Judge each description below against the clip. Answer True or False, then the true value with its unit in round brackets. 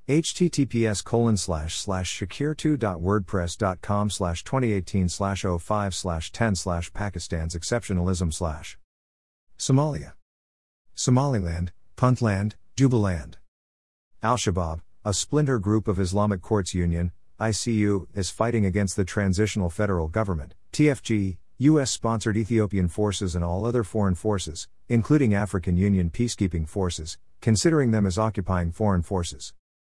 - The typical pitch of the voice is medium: False (100 Hz)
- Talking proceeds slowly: True (115 wpm)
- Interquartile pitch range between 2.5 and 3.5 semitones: False (4.1 semitones)